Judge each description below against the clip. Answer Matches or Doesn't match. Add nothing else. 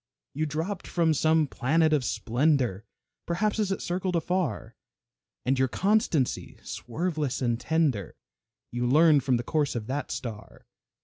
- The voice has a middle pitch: Matches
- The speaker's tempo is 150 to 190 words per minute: Doesn't match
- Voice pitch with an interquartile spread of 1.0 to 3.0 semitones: Doesn't match